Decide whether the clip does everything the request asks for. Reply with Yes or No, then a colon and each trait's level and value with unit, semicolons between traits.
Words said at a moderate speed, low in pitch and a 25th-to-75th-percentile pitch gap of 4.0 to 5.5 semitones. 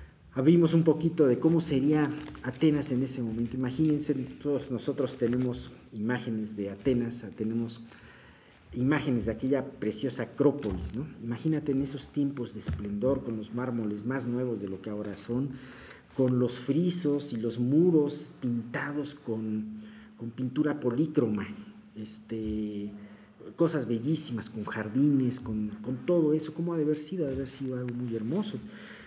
Yes: average, 150 wpm; low, 130 Hz; average, 4.5 semitones